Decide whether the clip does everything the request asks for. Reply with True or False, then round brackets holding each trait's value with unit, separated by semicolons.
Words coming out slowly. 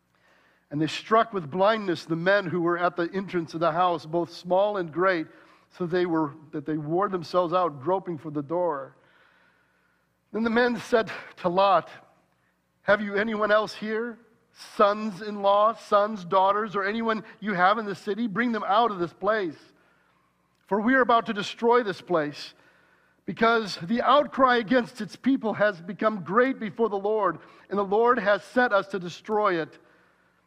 False (175 wpm)